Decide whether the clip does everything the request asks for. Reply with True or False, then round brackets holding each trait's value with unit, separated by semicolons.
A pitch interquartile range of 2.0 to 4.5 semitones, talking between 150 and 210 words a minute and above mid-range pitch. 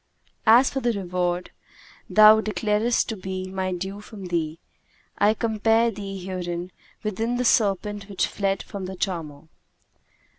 False (2.9 semitones; 140 wpm; 195 Hz)